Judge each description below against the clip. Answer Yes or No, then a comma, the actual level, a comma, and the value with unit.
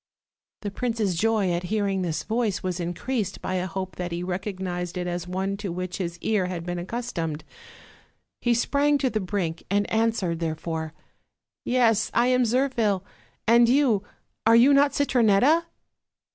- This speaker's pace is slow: No, average, 160 wpm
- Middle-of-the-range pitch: No, high, 200 Hz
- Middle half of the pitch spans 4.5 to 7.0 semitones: Yes, average, 4.8 semitones